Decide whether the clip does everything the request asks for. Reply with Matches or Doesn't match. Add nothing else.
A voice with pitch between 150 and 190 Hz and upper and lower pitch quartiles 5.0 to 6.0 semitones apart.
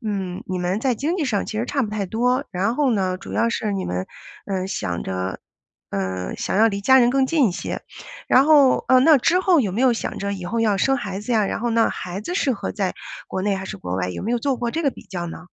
Doesn't match